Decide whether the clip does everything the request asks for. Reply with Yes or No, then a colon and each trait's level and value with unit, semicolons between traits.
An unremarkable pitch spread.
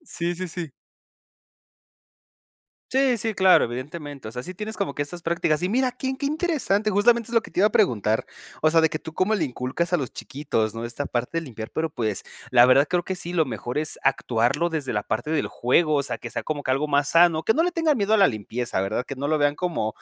No: wide, 6.9 semitones